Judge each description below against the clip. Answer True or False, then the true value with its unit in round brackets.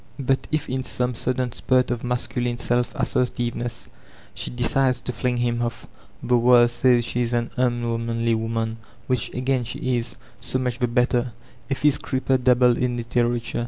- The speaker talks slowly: False (165 wpm)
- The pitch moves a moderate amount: False (1.2 semitones)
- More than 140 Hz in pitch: False (120 Hz)